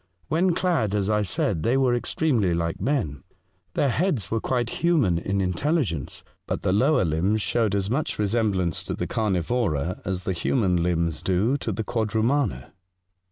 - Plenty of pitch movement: Yes, wide, 5.7 semitones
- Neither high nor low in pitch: No, low, 105 Hz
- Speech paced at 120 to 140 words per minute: No, average, 170 wpm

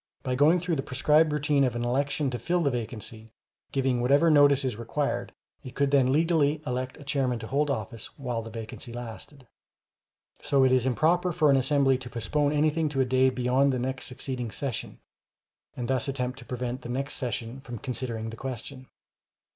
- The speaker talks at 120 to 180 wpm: No, average, 190 wpm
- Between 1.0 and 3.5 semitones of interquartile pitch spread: Yes, average, 2.7 semitones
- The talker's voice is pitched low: Yes, low, 130 Hz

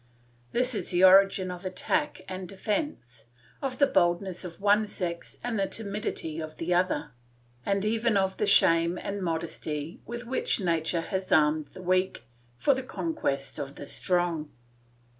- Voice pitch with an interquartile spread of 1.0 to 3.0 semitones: No, average, 4.0 semitones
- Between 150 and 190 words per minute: Yes, average, 160 wpm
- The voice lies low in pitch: No, medium, 185 Hz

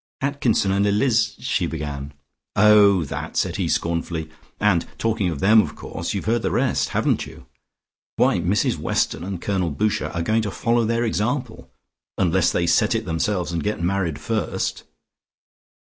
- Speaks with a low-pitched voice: Yes, low, 100 Hz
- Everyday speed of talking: Yes, average, 165 wpm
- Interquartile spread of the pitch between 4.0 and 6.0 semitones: Yes, average, 4.6 semitones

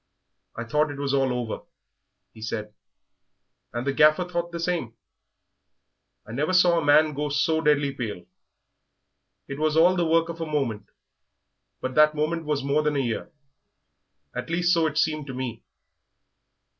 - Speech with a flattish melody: No, average, 3.7 semitones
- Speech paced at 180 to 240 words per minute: No, average, 165 wpm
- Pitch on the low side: No, medium, 150 Hz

